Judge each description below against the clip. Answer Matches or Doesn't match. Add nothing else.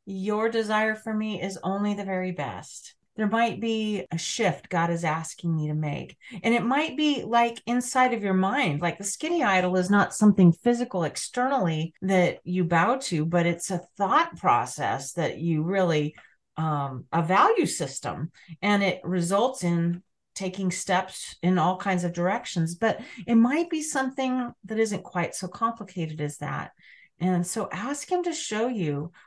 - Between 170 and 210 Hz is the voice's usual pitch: Matches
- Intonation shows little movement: Doesn't match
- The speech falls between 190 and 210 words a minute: Doesn't match